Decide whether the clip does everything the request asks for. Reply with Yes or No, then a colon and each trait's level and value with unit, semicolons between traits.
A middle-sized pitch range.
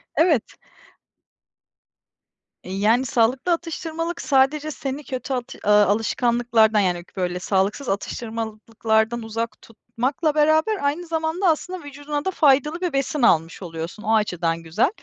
No: wide, 6.0 semitones